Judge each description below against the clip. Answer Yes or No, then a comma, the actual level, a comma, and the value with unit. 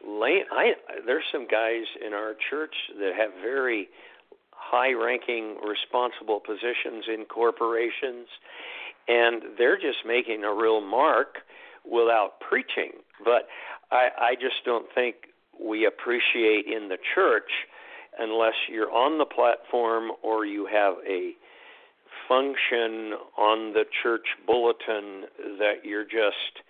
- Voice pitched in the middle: No, low, 115 Hz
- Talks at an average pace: No, slow, 120 wpm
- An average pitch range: No, narrow, 1.8 semitones